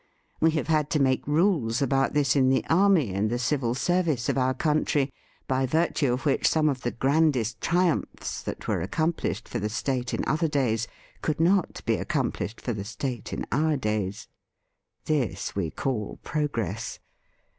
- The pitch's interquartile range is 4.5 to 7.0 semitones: Yes, average, 4.8 semitones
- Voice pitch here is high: No, low, 135 Hz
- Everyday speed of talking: Yes, average, 170 wpm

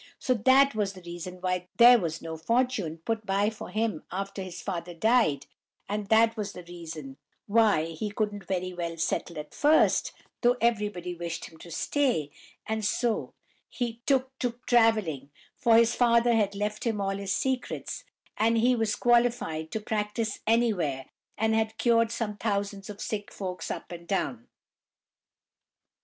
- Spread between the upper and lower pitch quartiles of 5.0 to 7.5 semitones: No, average, 4.6 semitones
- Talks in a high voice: Yes, high, 210 Hz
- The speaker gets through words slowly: No, average, 160 wpm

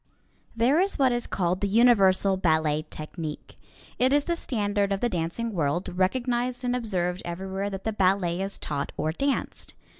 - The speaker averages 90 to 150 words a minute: No, average, 170 wpm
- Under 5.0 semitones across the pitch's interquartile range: No, wide, 5.5 semitones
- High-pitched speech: Yes, high, 195 Hz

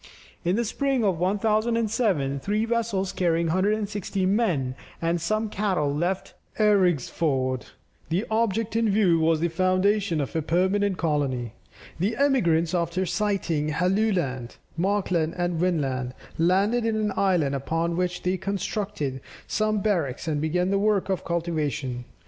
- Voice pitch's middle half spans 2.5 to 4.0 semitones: No, average, 4.5 semitones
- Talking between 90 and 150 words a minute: Yes, slow, 135 wpm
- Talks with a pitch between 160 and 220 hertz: Yes, medium, 185 Hz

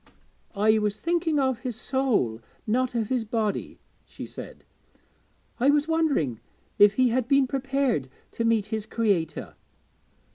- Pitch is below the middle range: No, high, 235 Hz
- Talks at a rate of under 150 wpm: Yes, average, 140 wpm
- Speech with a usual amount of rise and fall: Yes, average, 4.3 semitones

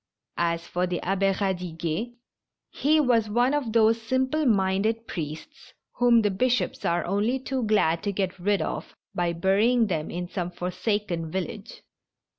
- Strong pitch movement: No, average, 4.8 semitones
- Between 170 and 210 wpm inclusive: No, average, 155 wpm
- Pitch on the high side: Yes, high, 200 Hz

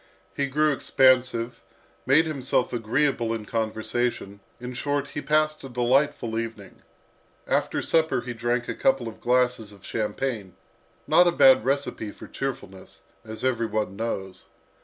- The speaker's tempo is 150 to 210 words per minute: No, average, 140 wpm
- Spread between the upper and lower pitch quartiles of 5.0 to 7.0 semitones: No, average, 3.4 semitones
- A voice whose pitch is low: Yes, low, 125 Hz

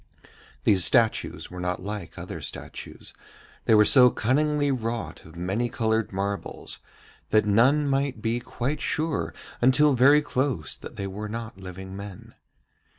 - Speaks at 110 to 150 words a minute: Yes, average, 145 wpm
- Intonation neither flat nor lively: Yes, average, 5.0 semitones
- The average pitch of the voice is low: Yes, low, 115 Hz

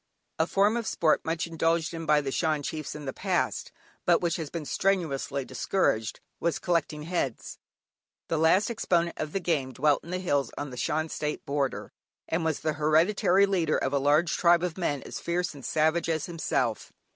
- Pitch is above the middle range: No, medium, 160 Hz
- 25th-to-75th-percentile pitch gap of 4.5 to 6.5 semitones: No, average, 2.9 semitones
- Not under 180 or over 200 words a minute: Yes, average, 190 wpm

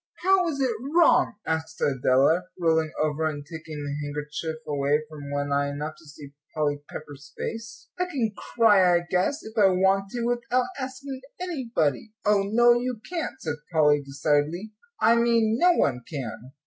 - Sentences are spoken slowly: No, average, 165 wpm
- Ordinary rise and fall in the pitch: No, wide, 8.2 semitones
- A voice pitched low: No, medium, 170 Hz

